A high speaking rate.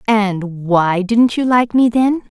No: average, 175 wpm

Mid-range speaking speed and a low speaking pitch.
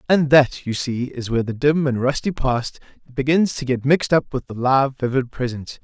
No: fast, 215 wpm; low, 130 Hz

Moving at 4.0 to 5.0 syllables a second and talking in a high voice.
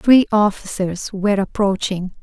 Yes: 4.4 syllables/s; high, 200 Hz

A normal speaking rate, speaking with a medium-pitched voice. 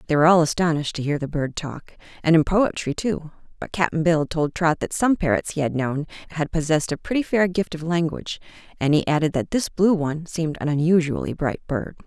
No: fast, 210 wpm; medium, 160 Hz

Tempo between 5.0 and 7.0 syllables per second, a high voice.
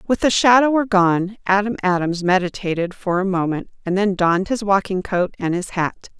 Yes: 5.2 syllables/s; high, 195 Hz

